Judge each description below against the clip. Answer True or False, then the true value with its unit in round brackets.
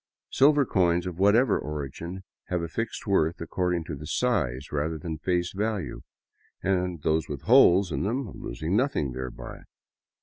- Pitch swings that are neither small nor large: True (4.3 semitones)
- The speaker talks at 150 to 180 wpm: False (140 wpm)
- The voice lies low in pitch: True (90 Hz)